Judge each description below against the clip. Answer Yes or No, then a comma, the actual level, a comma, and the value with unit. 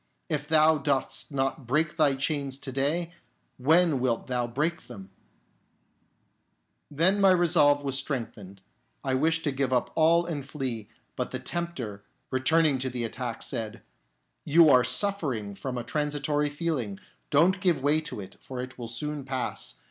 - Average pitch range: Yes, average, 4.0 semitones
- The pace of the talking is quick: No, average, 165 wpm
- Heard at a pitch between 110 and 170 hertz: Yes, medium, 140 Hz